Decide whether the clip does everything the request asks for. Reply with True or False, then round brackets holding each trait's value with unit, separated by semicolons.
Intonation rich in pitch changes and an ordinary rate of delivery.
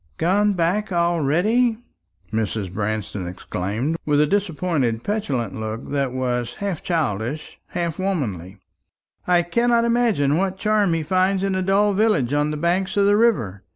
True (8.2 semitones; 150 wpm)